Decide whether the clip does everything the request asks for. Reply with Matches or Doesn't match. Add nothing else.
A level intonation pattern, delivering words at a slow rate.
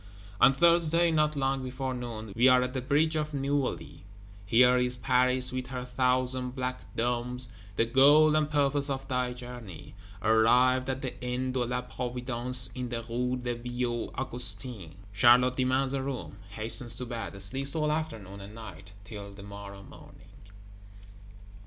Doesn't match